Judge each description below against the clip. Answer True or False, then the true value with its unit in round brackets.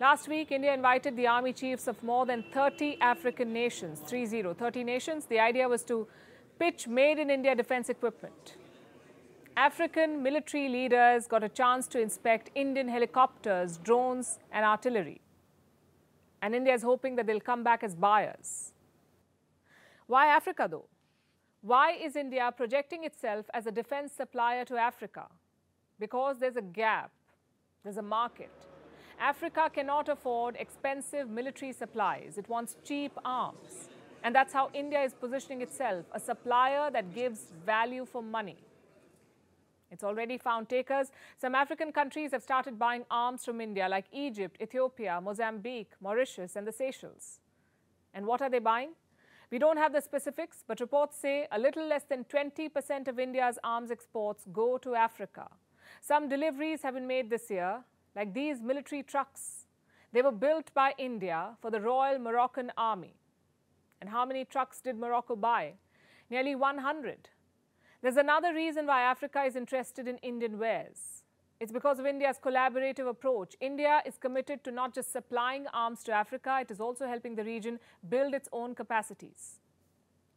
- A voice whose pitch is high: True (250 Hz)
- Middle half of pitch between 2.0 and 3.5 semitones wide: True (3.0 semitones)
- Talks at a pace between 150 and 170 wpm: True (155 wpm)